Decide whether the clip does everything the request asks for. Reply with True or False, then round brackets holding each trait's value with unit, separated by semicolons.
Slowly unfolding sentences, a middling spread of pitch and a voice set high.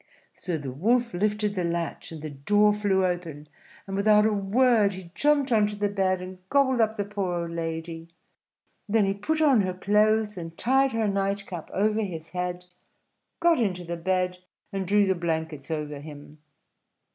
False (180 wpm; 3.7 semitones; 195 Hz)